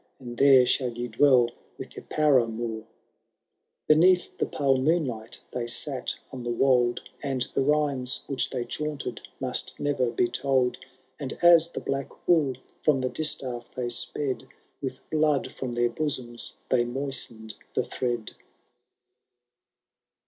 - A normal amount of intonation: Yes, average, 3.0 semitones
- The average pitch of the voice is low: Yes, low, 130 Hz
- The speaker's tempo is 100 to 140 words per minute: Yes, slow, 135 wpm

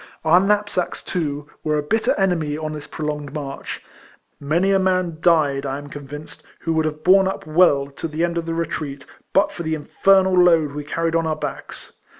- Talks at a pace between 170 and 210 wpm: Yes, average, 195 wpm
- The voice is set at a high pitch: No, medium, 160 Hz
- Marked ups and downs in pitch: No, average, 3.3 semitones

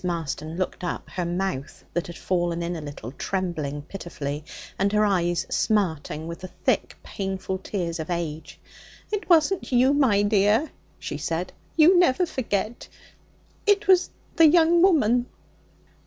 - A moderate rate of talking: Yes, average, 145 wpm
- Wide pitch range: Yes, wide, 6.9 semitones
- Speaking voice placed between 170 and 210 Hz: Yes, high, 190 Hz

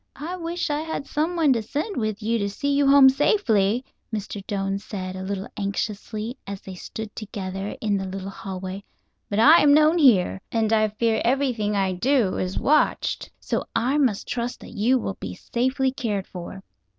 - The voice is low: No, high, 220 Hz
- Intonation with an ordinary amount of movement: No, wide, 5.7 semitones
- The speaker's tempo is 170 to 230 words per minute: Yes, average, 185 wpm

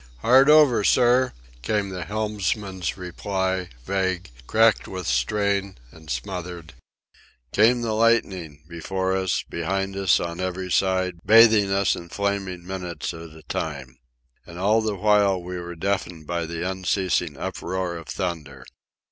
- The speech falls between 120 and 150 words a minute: Yes, average, 140 wpm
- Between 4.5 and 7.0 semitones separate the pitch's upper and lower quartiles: No, average, 2.9 semitones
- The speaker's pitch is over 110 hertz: No, very low, 95 Hz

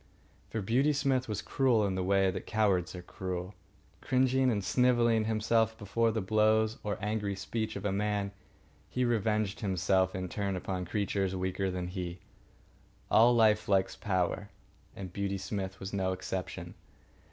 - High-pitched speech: No, low, 100 Hz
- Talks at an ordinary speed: Yes, average, 155 wpm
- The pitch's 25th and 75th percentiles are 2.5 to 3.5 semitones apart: Yes, average, 2.9 semitones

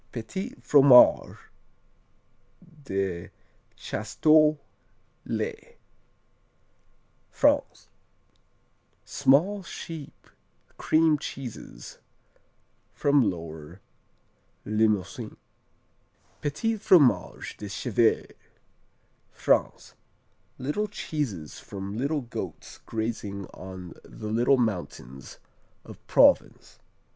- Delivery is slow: Yes, slow, 65 wpm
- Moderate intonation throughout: No, wide, 7.4 semitones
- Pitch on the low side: Yes, low, 120 Hz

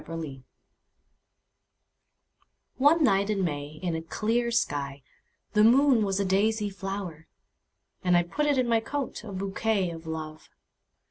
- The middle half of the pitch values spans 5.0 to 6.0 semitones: Yes, wide, 5.5 semitones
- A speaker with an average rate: No, slow, 125 wpm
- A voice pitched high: Yes, high, 195 Hz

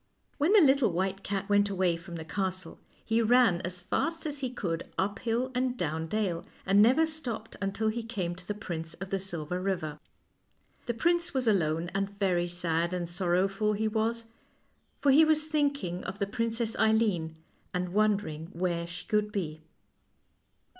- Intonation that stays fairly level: No, average, 4.7 semitones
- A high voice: Yes, high, 200 Hz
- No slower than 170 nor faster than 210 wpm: Yes, average, 175 wpm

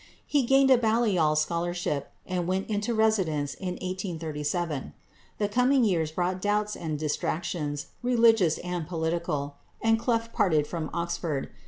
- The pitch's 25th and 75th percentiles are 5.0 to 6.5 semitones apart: Yes, wide, 5.6 semitones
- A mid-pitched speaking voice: Yes, medium, 180 Hz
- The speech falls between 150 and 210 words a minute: No, slow, 135 wpm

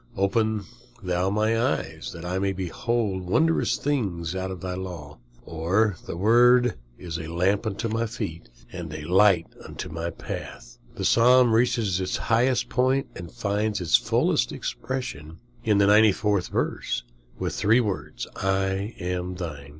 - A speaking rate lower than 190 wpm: Yes, average, 145 wpm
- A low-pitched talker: Yes, very low, 95 Hz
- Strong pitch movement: No, average, 4.3 semitones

